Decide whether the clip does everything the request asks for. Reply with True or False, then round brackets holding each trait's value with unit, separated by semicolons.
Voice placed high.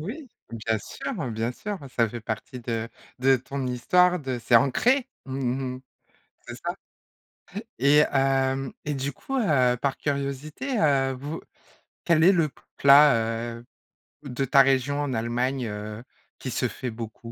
False (135 Hz)